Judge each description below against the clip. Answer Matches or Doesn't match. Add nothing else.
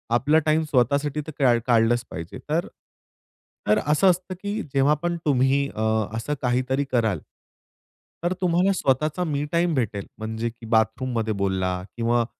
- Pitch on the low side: Matches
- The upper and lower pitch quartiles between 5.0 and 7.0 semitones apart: Matches